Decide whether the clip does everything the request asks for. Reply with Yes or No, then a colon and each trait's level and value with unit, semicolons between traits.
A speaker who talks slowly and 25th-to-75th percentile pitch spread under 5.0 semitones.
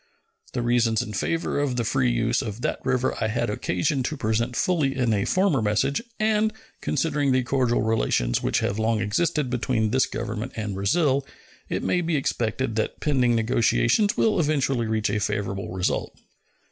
No: average, 170 wpm; average, 4.2 semitones